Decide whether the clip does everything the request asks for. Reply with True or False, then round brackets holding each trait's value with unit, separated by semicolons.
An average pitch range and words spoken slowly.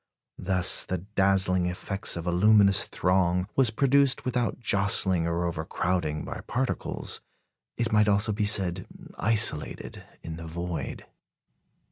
True (3.4 semitones; 125 wpm)